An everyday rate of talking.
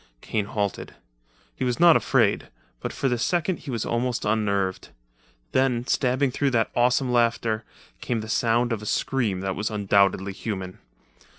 Yes: average, 160 wpm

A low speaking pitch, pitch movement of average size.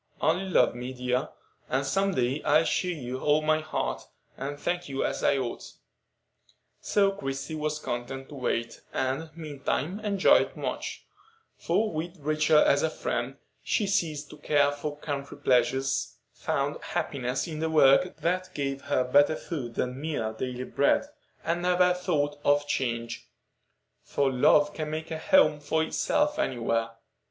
No: medium, 145 Hz; average, 3.3 semitones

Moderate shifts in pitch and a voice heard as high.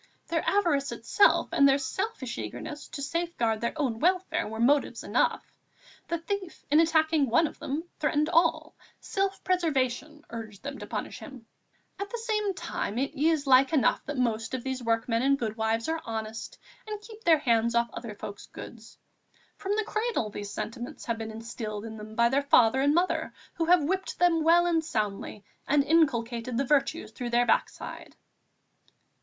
No: wide, 6.2 semitones; very high, 275 Hz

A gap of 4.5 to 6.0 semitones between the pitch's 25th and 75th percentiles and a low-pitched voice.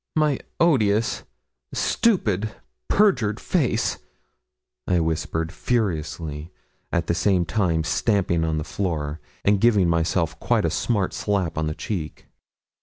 Yes: average, 5.0 semitones; very low, 90 Hz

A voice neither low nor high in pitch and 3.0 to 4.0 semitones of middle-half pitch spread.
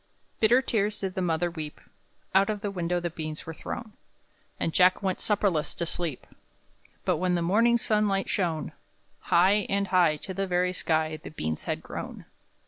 Yes: medium, 180 Hz; average, 3.3 semitones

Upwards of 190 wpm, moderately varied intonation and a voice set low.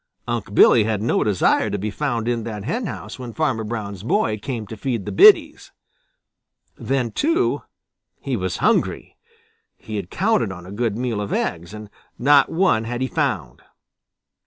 No: average, 165 wpm; average, 4.0 semitones; low, 115 Hz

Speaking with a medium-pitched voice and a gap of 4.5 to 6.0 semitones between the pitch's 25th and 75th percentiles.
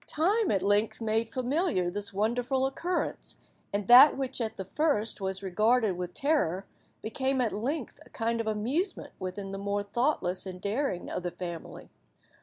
No: high, 220 Hz; wide, 5.4 semitones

